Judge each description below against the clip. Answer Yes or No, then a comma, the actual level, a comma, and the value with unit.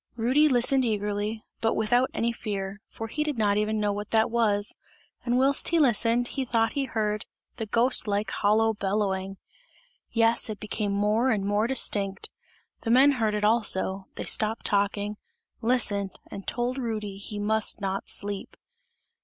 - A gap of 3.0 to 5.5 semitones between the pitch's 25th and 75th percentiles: No, narrow, 2.5 semitones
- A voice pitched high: Yes, high, 215 Hz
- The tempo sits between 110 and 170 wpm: Yes, average, 160 wpm